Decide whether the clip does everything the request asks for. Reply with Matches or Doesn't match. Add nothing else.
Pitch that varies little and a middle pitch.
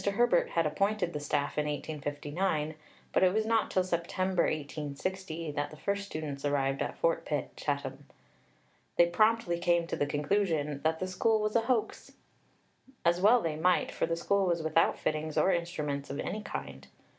Doesn't match